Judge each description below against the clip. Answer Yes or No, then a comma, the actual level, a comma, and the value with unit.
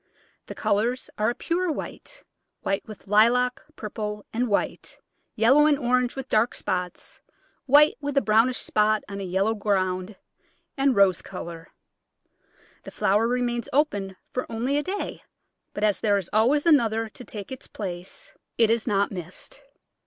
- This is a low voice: No, high, 225 Hz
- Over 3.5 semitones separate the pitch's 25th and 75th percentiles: Yes, average, 4.0 semitones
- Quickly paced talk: No, average, 155 wpm